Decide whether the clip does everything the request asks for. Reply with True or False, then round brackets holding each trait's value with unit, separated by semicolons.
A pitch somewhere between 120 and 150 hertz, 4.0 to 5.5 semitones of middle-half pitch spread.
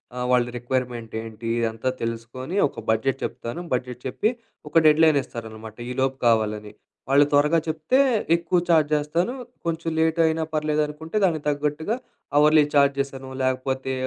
True (140 Hz; 4.4 semitones)